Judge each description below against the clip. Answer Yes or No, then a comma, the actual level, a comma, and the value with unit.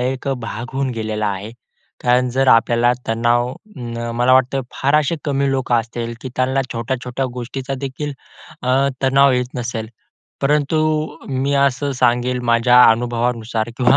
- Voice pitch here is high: No, low, 125 Hz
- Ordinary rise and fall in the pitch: No, narrow, 2.2 semitones